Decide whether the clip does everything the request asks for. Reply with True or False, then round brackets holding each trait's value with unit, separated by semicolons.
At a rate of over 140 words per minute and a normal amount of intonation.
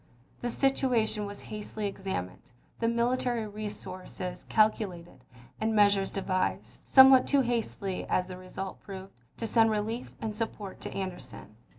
False (135 wpm; 3.3 semitones)